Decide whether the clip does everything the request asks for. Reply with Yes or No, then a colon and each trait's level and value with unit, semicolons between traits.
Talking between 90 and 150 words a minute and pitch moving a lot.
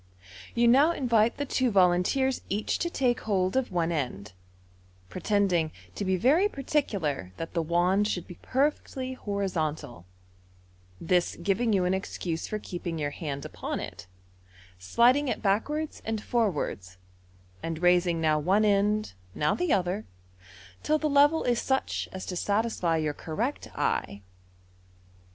Yes: average, 140 wpm; wide, 6.5 semitones